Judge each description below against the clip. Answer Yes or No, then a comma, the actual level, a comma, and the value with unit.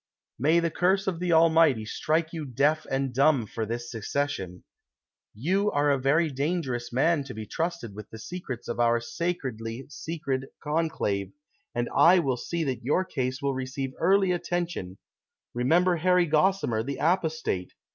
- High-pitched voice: No, medium, 145 Hz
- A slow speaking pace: No, average, 165 wpm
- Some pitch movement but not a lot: No, wide, 5.7 semitones